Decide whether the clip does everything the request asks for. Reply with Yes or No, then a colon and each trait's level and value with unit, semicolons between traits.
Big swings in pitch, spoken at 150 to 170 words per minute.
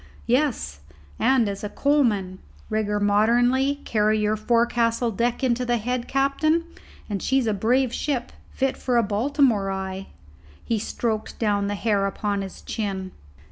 No: average, 3.6 semitones; average, 155 wpm